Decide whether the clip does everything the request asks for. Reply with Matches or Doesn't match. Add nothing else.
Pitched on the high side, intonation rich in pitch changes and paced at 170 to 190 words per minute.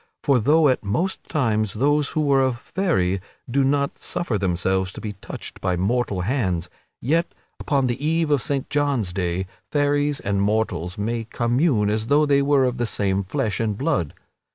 Doesn't match